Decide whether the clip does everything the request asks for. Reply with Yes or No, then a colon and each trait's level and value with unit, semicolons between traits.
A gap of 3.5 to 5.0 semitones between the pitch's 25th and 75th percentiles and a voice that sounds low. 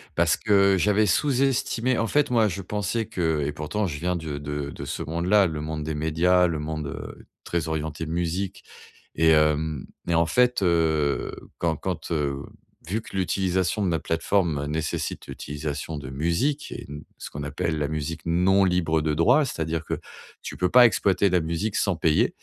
Yes: average, 4.0 semitones; very low, 85 Hz